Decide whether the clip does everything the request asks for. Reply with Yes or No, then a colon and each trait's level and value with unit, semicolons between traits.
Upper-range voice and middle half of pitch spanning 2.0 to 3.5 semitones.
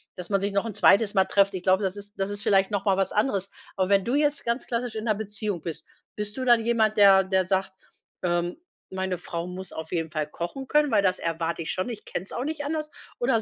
Yes: high, 200 Hz; average, 3.2 semitones